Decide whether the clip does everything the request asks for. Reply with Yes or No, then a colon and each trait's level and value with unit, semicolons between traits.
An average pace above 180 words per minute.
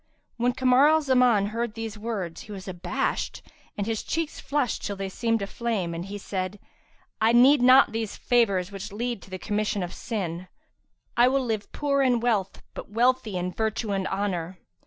Yes: average, 190 wpm